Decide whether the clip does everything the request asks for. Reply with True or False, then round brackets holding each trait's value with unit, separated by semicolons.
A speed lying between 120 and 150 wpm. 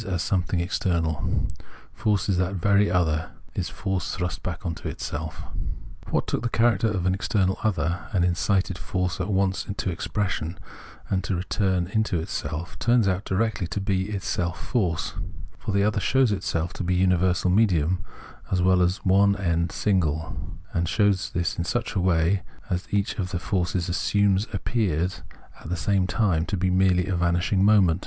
False (170 wpm)